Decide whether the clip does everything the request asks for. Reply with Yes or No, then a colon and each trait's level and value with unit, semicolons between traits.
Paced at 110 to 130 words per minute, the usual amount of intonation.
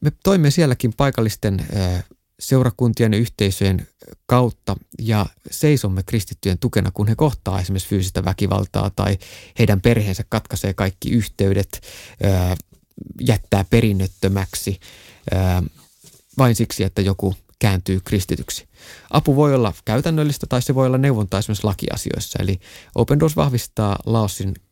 Yes: average, 115 wpm; average, 3.9 semitones